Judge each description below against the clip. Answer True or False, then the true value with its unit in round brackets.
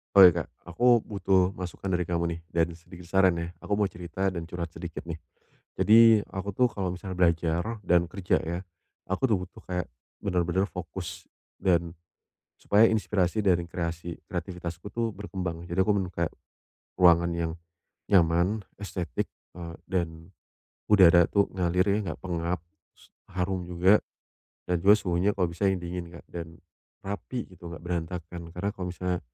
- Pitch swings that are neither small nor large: False (2.2 semitones)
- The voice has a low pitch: True (90 Hz)